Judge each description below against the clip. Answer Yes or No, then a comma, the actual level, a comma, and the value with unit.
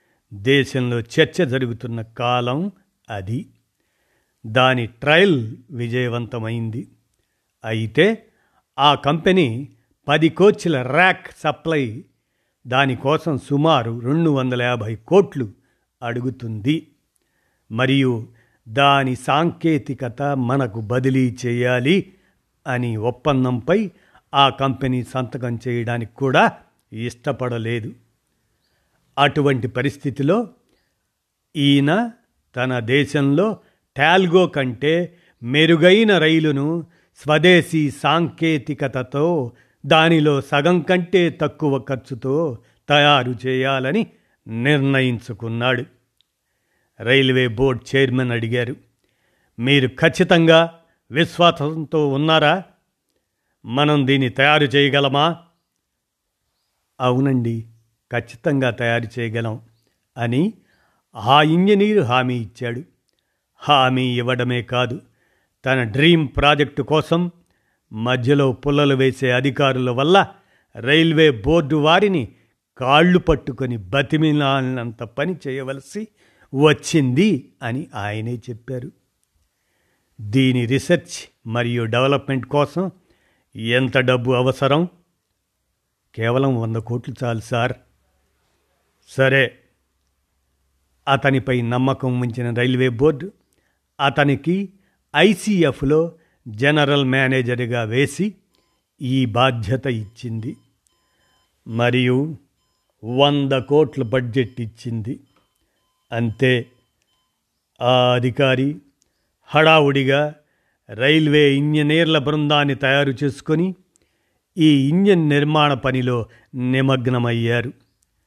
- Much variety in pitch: No, average, 3.8 semitones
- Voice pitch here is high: No, low, 135 Hz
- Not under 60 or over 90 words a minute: Yes, average, 75 wpm